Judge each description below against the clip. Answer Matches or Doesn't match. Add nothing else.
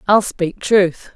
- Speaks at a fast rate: Doesn't match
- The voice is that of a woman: Matches